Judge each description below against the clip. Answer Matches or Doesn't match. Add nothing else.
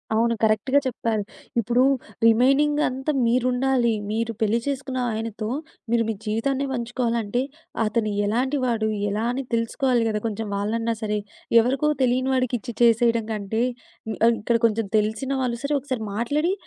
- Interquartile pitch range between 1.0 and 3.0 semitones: Matches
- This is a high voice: Matches